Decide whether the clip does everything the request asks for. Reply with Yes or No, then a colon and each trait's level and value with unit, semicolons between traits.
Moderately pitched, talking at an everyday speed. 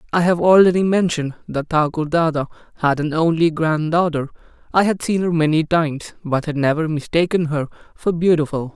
Yes: medium, 160 Hz; average, 170 wpm